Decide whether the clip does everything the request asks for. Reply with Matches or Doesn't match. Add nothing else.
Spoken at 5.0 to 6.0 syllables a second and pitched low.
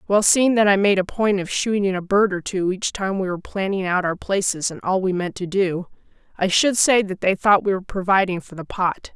Doesn't match